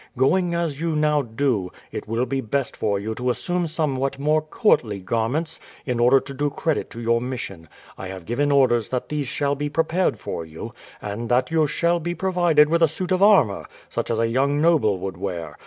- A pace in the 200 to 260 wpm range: Yes, fast, 205 wpm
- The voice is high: No, low, 135 Hz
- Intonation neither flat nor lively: No, wide, 5.8 semitones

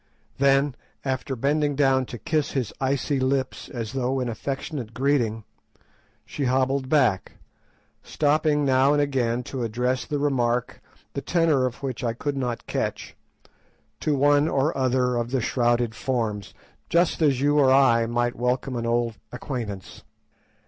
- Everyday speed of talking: Yes, average, 150 wpm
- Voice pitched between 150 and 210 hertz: No, low, 130 Hz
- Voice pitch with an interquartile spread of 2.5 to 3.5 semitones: Yes, average, 2.8 semitones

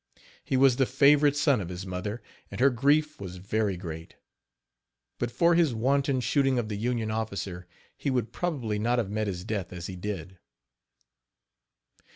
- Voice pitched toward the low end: Yes, low, 110 Hz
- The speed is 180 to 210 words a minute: No, average, 170 wpm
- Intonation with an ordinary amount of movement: No, wide, 5.8 semitones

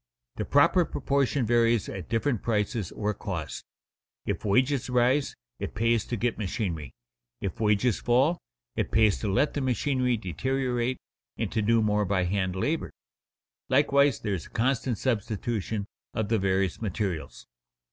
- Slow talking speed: No, average, 145 wpm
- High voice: No, low, 115 Hz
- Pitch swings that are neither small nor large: Yes, average, 4.3 semitones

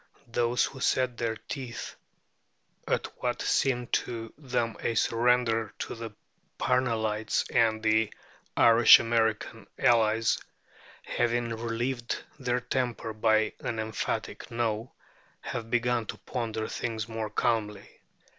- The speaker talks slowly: Yes, slow, 115 wpm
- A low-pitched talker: Yes, low, 115 Hz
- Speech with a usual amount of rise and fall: No, narrow, 1.6 semitones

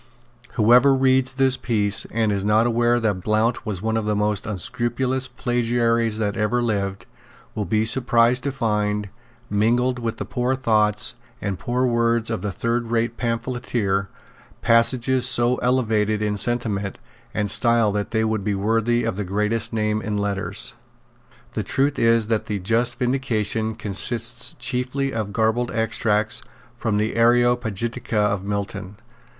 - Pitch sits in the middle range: No, low, 115 Hz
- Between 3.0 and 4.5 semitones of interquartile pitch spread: No, narrow, 2.5 semitones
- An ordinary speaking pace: Yes, average, 145 wpm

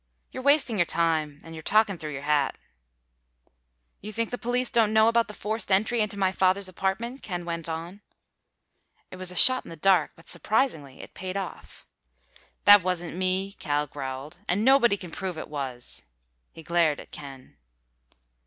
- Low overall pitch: No, medium, 185 Hz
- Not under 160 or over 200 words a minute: Yes, average, 175 wpm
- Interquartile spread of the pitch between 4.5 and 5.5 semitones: Yes, average, 5.0 semitones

